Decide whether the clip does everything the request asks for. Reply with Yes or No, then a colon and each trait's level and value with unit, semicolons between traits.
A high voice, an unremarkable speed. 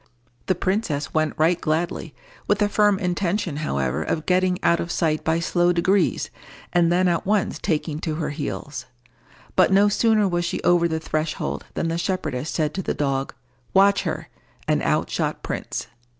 No: medium, 170 Hz; average, 175 wpm